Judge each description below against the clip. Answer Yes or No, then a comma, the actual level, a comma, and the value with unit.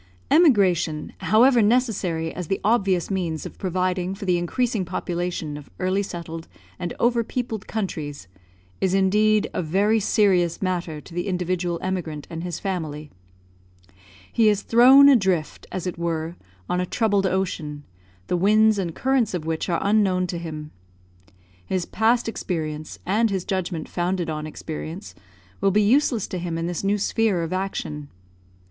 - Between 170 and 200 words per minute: No, average, 155 wpm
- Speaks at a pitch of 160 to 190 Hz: Yes, medium, 185 Hz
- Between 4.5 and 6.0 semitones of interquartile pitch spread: No, average, 3.8 semitones